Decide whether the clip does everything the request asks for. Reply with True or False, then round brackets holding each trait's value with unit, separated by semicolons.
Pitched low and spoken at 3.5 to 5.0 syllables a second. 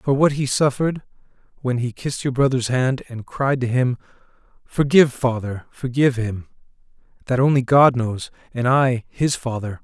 True (125 Hz; 4.9 syllables/s)